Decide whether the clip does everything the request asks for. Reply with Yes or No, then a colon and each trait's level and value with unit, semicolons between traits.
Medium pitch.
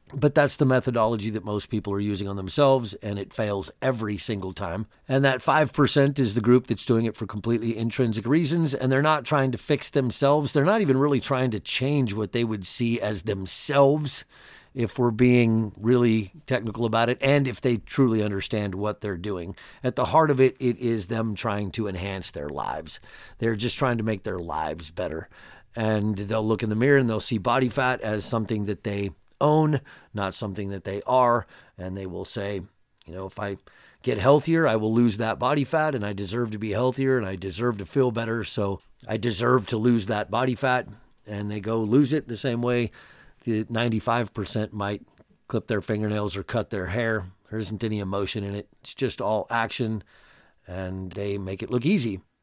No: low, 115 Hz